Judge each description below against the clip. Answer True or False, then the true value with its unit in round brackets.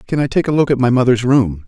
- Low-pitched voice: True (125 Hz)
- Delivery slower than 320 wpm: False (325 wpm)